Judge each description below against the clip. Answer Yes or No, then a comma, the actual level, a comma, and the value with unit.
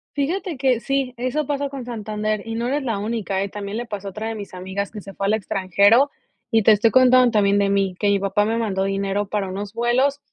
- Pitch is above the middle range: Yes, high, 215 Hz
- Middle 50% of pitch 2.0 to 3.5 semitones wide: No, average, 3.9 semitones